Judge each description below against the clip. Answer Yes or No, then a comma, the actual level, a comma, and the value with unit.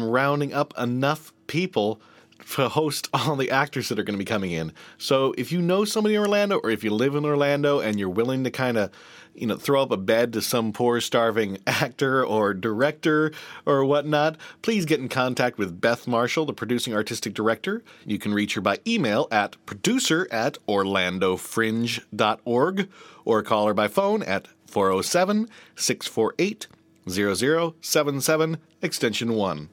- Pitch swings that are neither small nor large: No, wide, 6.1 semitones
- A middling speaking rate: Yes, average, 160 wpm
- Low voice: Yes, low, 125 Hz